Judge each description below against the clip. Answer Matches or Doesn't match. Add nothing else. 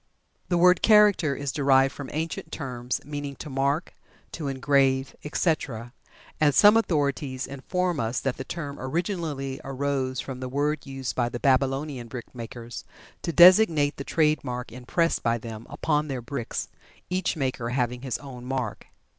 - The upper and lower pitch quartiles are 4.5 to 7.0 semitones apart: Doesn't match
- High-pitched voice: Doesn't match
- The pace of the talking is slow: Doesn't match